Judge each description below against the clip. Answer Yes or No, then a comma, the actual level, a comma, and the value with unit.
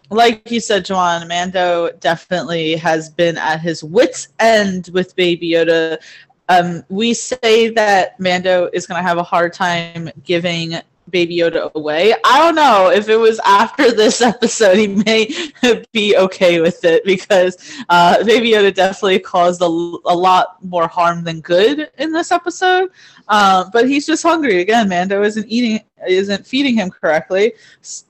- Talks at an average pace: Yes, average, 160 wpm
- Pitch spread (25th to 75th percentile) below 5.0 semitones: Yes, average, 4.6 semitones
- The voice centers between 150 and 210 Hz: Yes, medium, 185 Hz